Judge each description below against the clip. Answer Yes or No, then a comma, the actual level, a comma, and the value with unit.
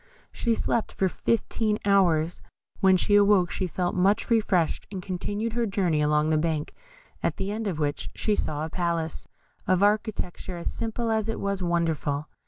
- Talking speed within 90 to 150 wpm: No, average, 175 wpm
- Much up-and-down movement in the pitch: No, average, 4.2 semitones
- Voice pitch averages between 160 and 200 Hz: Yes, medium, 185 Hz